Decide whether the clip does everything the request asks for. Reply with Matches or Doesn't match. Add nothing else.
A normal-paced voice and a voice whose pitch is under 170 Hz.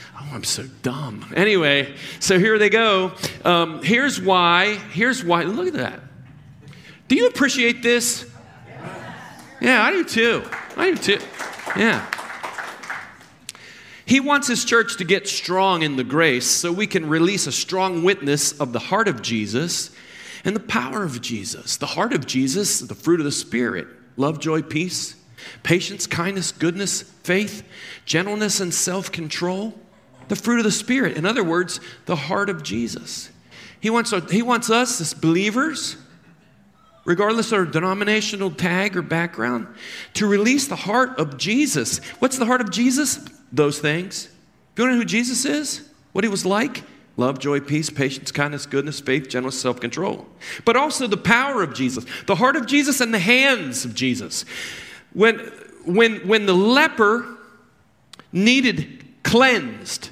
Doesn't match